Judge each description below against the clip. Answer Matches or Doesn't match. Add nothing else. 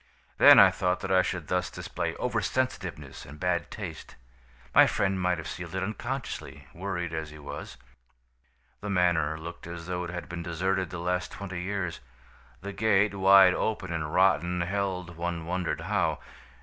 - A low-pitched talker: Matches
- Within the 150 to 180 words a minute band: Matches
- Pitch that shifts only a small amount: Matches